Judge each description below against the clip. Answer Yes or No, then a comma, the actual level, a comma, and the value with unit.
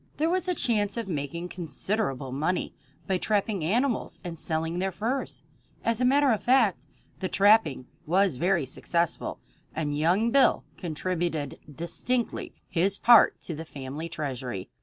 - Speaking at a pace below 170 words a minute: Yes, average, 145 wpm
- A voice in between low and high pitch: Yes, medium, 180 Hz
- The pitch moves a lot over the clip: Yes, wide, 5.9 semitones